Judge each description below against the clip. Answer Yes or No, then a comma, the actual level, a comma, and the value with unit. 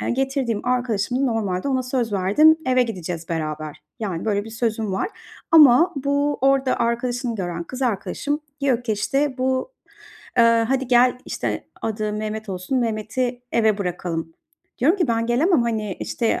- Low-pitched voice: No, high, 235 Hz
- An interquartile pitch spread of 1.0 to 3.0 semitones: No, average, 3.9 semitones